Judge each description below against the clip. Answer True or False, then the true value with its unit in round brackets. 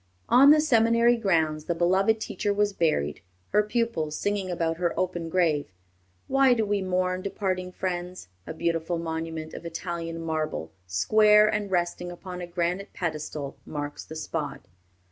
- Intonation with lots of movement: False (4.0 semitones)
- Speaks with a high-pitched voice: False (175 Hz)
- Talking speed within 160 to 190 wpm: False (150 wpm)